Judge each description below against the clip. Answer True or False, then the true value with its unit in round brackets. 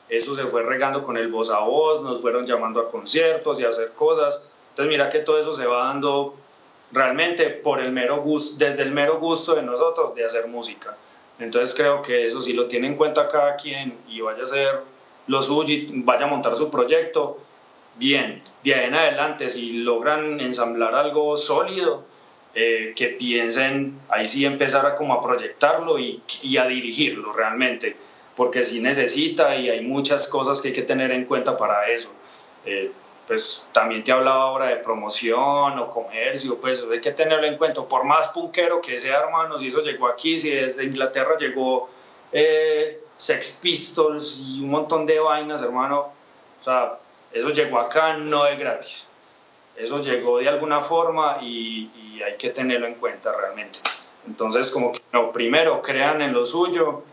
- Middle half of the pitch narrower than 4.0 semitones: False (4.5 semitones)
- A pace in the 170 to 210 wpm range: True (180 wpm)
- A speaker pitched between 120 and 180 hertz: True (140 Hz)